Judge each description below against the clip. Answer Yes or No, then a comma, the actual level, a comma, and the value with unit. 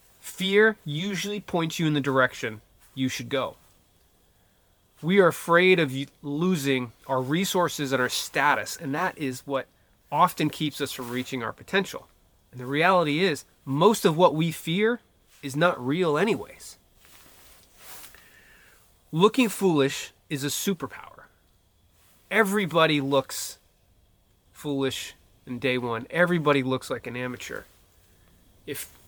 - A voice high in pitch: No, low, 135 Hz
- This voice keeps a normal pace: No, slow, 125 wpm